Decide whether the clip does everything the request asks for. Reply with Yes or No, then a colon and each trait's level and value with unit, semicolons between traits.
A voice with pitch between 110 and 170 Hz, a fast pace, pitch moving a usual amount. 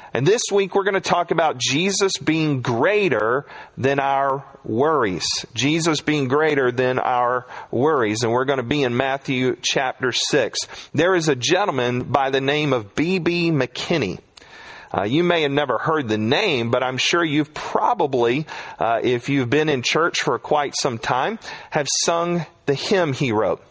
No: medium, 140 Hz; average, 170 wpm; average, 4.2 semitones